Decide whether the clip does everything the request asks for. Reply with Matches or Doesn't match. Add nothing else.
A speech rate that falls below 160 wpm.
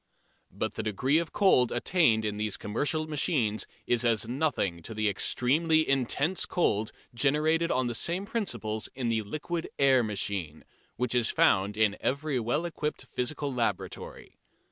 Matches